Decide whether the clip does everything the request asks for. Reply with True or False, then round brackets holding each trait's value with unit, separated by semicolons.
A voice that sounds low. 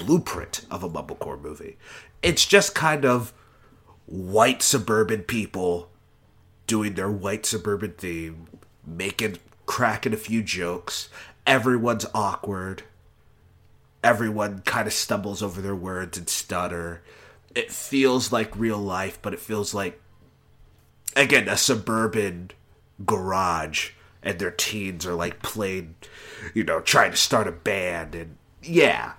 True (100 Hz)